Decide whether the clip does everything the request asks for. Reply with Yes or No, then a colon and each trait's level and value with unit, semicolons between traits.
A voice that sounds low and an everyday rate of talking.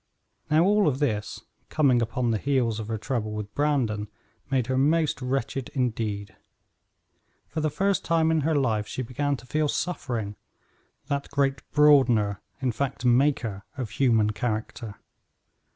Yes: low, 130 Hz; average, 150 wpm